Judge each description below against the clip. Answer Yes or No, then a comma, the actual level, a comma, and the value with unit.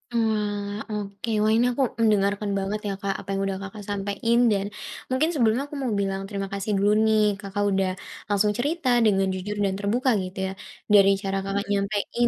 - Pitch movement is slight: Yes, narrow, 2.0 semitones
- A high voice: Yes, high, 205 Hz